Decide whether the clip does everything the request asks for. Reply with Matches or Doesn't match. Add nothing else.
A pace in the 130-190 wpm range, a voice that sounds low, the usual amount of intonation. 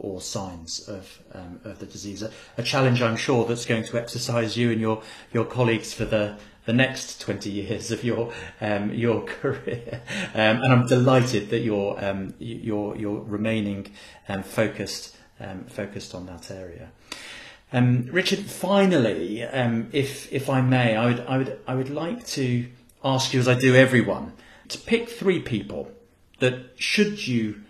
Matches